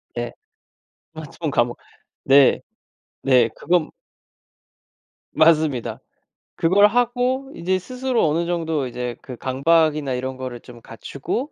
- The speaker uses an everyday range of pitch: No, wide, 6.0 semitones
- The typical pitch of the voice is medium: Yes, medium, 155 Hz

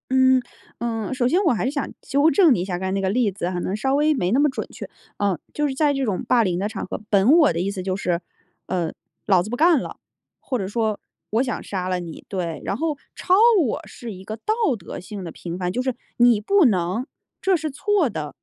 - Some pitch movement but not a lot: No, wide, 6.3 semitones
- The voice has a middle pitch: No, high, 220 Hz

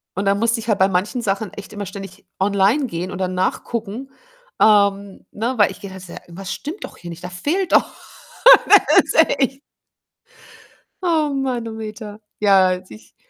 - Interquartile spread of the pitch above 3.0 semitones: Yes, average, 3.7 semitones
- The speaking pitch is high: Yes, high, 205 Hz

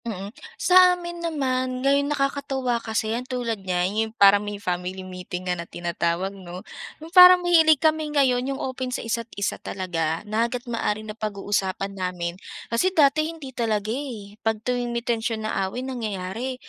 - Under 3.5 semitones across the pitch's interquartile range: No, average, 5.3 semitones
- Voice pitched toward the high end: Yes, high, 230 Hz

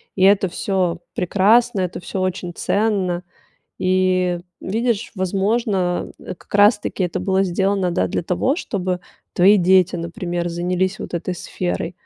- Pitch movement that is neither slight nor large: No, narrow, 2.0 semitones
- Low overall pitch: No, medium, 185 Hz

